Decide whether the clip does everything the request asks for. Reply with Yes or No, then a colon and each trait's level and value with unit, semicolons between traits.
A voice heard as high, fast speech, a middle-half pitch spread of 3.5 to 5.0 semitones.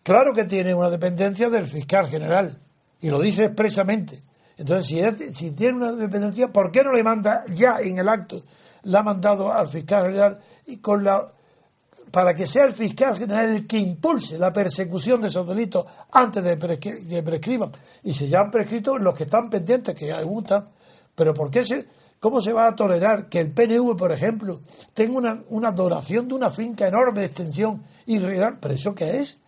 Yes: high, 205 Hz; fast, 205 wpm; average, 4.3 semitones